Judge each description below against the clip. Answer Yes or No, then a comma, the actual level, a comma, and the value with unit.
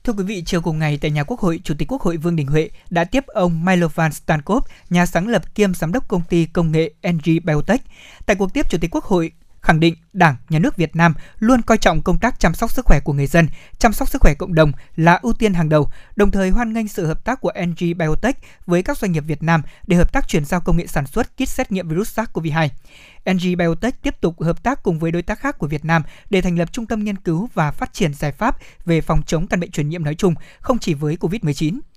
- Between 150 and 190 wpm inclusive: No, fast, 265 wpm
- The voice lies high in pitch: No, medium, 175 Hz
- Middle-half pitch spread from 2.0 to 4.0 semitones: No, average, 4.4 semitones